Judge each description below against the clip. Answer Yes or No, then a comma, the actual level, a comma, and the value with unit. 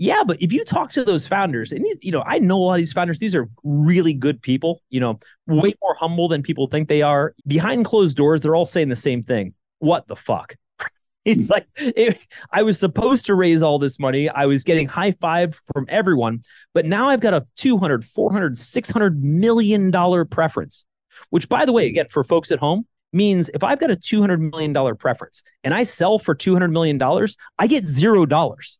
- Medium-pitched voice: Yes, medium, 170 Hz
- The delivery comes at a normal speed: No, fast, 215 wpm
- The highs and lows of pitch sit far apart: Yes, wide, 5.8 semitones